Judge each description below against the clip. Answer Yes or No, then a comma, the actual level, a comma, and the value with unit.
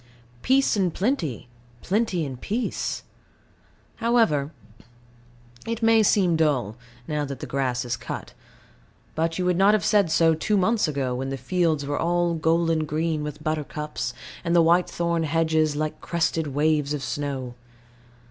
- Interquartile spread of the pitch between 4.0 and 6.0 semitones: No, average, 3.6 semitones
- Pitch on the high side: No, medium, 160 Hz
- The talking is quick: No, average, 145 wpm